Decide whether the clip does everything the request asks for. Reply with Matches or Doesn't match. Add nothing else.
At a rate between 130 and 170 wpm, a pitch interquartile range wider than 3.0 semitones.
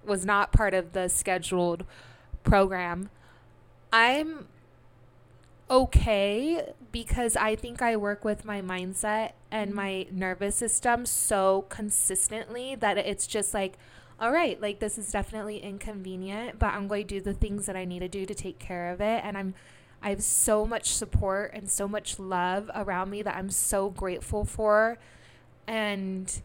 Doesn't match